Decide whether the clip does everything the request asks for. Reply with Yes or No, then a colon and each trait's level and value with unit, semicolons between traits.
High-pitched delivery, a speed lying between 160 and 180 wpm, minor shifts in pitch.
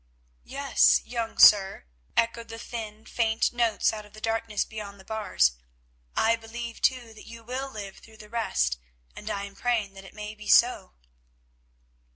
Yes: high, 220 Hz; average, 170 wpm; narrow, 2.1 semitones